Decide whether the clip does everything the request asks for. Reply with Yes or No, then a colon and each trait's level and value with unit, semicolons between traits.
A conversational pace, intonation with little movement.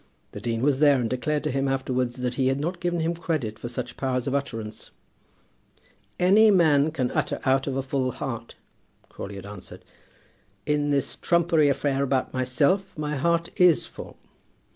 No: average, 175 wpm; average, 3.4 semitones